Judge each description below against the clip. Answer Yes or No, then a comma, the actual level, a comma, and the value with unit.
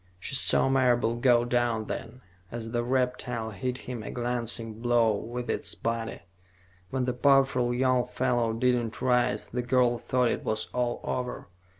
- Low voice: Yes, low, 120 Hz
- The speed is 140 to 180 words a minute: Yes, average, 165 wpm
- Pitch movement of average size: No, narrow, 1.4 semitones